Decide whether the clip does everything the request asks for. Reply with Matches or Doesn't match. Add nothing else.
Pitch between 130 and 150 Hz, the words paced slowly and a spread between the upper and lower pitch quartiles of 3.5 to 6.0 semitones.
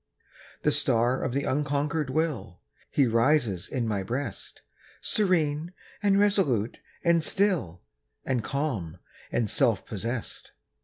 Matches